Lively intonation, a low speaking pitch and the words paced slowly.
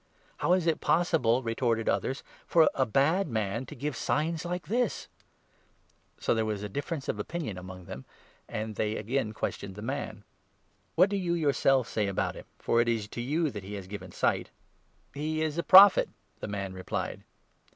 No: wide, 7.2 semitones; low, 125 Hz; fast, 205 wpm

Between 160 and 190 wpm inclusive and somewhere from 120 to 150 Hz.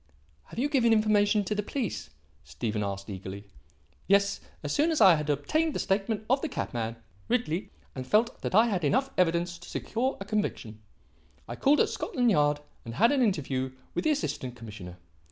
No: average, 185 wpm; high, 195 Hz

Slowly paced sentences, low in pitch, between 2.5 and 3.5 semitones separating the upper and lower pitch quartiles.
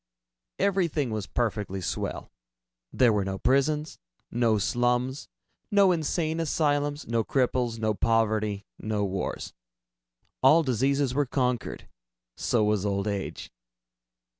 No: slow, 115 wpm; low, 120 Hz; average, 5.2 semitones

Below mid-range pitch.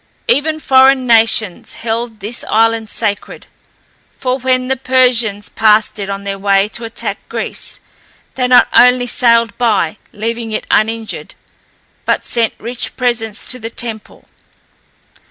No: high, 230 Hz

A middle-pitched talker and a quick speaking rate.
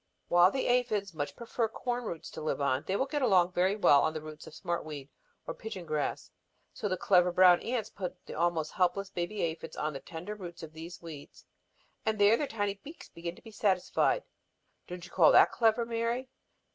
Yes: medium, 180 Hz; fast, 210 wpm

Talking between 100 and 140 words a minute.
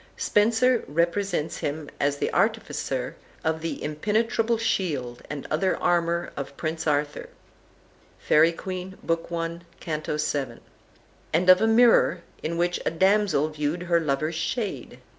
Yes: slow, 135 wpm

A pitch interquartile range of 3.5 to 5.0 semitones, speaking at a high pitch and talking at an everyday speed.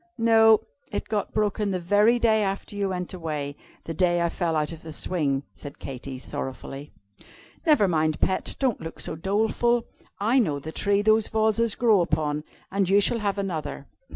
No: wide, 5.4 semitones; high, 195 Hz; average, 180 wpm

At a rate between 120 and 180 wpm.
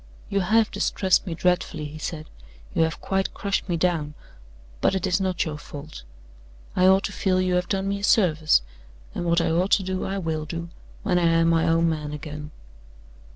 No: average, 200 wpm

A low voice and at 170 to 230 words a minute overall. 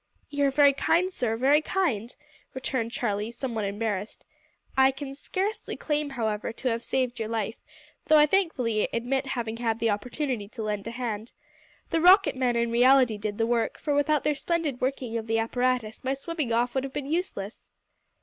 No: very high, 250 Hz; average, 185 wpm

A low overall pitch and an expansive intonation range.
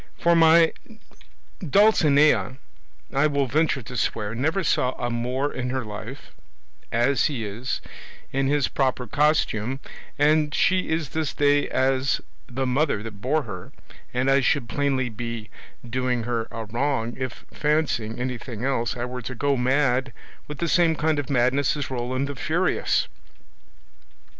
No: low, 130 Hz; average, 3.4 semitones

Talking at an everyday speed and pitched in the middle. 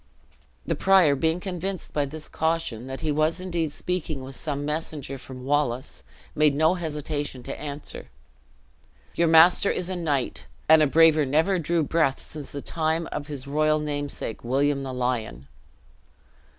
Yes: average, 155 wpm; medium, 150 Hz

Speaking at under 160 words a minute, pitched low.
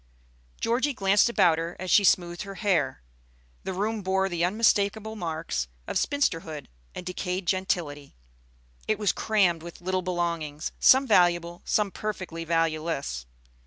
No: slow, 135 wpm; medium, 180 Hz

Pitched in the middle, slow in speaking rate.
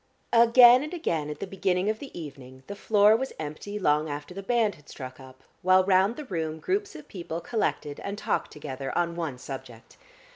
No: medium, 180 Hz; average, 195 wpm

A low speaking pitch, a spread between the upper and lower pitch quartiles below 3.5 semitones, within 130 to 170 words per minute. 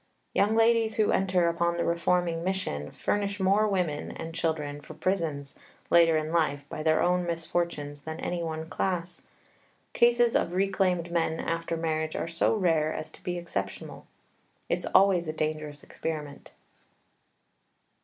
No: medium, 170 Hz; average, 2.8 semitones; average, 145 wpm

